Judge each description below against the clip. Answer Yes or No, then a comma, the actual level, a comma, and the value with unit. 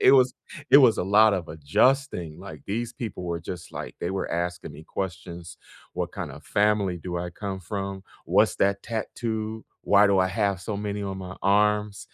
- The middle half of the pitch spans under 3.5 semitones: Yes, average, 3.1 semitones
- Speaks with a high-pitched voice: No, low, 100 Hz